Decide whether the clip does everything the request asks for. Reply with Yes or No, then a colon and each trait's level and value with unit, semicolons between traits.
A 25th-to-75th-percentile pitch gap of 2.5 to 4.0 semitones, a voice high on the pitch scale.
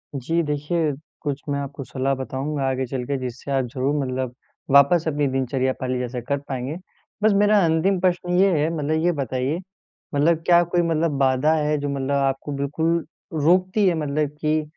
No: average, 3.5 semitones; medium, 145 Hz